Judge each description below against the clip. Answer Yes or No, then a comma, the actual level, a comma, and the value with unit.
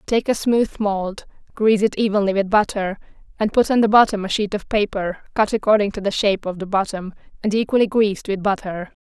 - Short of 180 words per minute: No, fast, 205 wpm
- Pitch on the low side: No, high, 205 Hz